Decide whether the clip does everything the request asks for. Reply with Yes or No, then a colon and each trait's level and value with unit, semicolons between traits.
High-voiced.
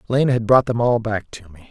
No: low, 115 Hz